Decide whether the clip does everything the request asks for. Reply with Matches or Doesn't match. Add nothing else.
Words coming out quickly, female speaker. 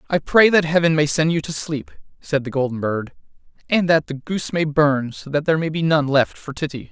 Doesn't match